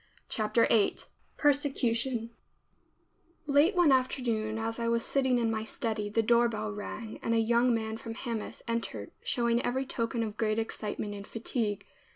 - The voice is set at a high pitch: Yes, high, 230 Hz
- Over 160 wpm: No, average, 155 wpm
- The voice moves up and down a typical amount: No, narrow, 1.9 semitones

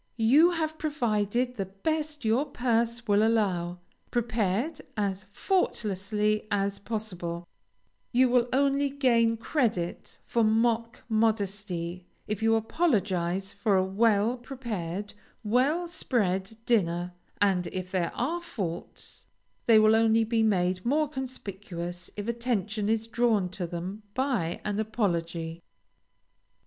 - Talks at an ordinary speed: No, slow, 120 wpm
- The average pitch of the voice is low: No, high, 215 Hz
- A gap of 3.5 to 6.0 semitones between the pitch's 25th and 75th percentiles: Yes, average, 4.2 semitones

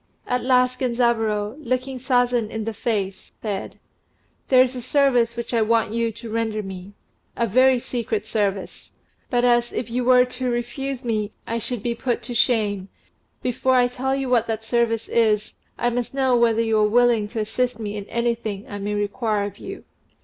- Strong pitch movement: No, narrow, 2.5 semitones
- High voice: Yes, high, 235 Hz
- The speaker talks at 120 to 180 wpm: No, average, 190 wpm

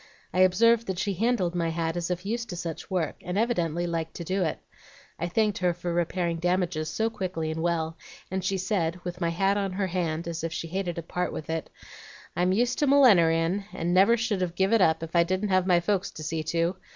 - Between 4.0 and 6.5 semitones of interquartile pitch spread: No, narrow, 2.6 semitones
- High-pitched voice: No, medium, 180 Hz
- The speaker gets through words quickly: Yes, fast, 235 wpm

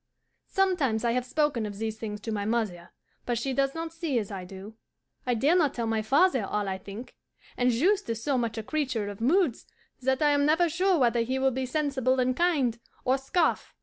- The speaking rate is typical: No, fast, 215 wpm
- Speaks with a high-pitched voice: Yes, very high, 250 Hz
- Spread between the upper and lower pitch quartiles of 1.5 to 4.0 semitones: No, average, 4.9 semitones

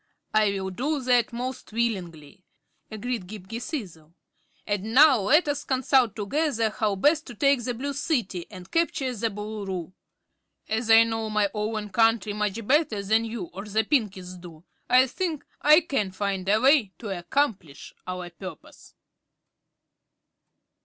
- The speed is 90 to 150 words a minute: Yes, average, 145 wpm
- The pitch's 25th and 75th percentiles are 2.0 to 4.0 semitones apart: No, average, 4.8 semitones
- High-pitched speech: Yes, high, 220 Hz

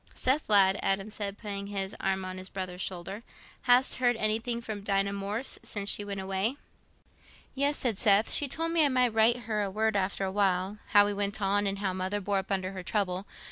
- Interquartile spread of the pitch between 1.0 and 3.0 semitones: Yes, narrow, 2.4 semitones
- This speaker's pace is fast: Yes, fast, 210 wpm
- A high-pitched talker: Yes, high, 200 Hz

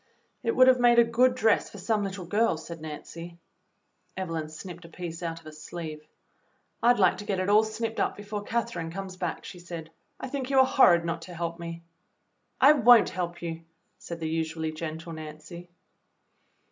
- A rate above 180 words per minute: Yes, average, 190 wpm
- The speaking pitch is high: No, medium, 175 Hz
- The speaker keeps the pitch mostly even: No, average, 4.8 semitones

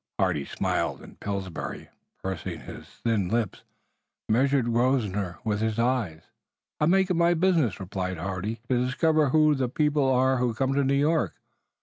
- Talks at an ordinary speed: Yes, average, 155 wpm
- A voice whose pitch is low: Yes, low, 125 Hz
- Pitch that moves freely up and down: Yes, wide, 5.8 semitones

